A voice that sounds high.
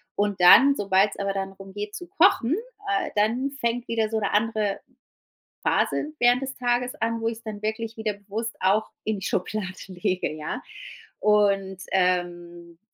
Yes: high, 210 Hz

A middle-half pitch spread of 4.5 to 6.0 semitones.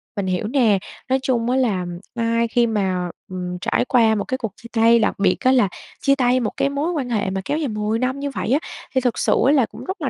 No: average, 3.8 semitones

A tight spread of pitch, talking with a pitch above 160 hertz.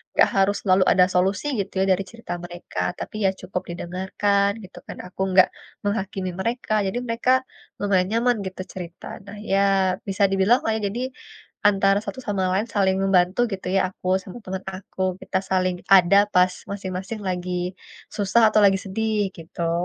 Yes: narrow, 1.8 semitones; high, 190 Hz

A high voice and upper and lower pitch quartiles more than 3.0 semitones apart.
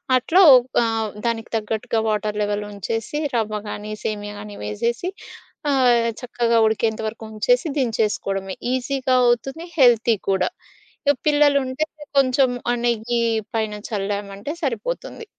Yes: high, 230 Hz; average, 3.4 semitones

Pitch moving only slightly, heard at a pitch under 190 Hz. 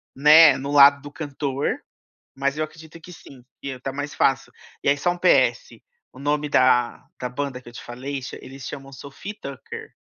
Yes: narrow, 1.8 semitones; medium, 140 Hz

